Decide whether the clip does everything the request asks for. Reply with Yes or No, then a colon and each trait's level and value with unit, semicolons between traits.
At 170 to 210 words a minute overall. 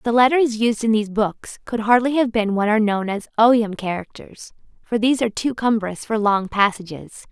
Yes: average, 195 wpm